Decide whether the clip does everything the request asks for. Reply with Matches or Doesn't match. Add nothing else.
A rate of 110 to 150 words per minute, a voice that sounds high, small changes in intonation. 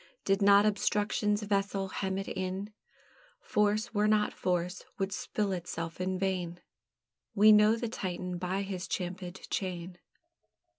Matches